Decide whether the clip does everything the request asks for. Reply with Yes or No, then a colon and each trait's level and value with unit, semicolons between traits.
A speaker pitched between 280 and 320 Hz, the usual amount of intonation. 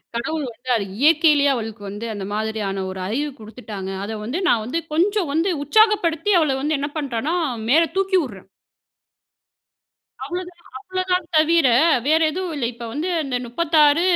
No: very high, 290 Hz; wide, 6.9 semitones